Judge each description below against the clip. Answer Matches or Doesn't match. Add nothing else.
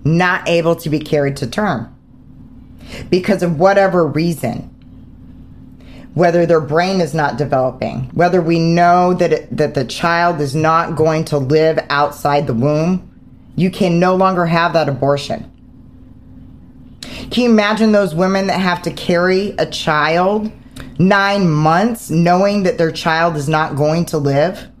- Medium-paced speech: Matches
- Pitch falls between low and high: Matches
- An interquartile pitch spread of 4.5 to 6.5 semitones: Doesn't match